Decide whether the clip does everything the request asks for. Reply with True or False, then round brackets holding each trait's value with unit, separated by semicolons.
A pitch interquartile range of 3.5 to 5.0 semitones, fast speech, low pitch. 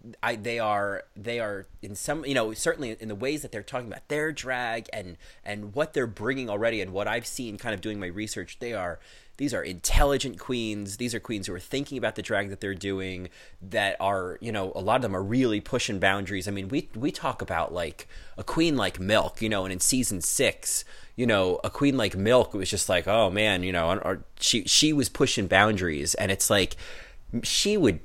True (4.2 semitones; 225 wpm; 110 Hz)